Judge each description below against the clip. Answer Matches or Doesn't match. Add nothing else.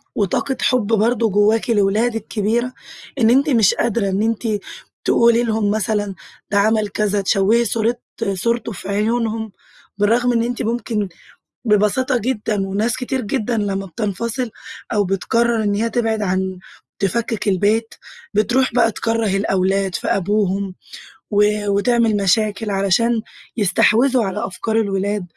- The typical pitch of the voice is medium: Doesn't match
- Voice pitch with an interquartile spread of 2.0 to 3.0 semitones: Matches